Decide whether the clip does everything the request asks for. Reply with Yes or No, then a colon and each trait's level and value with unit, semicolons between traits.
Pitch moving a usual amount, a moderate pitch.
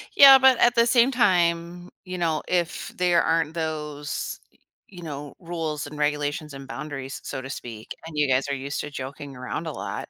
Yes: average, 3.4 semitones; medium, 155 Hz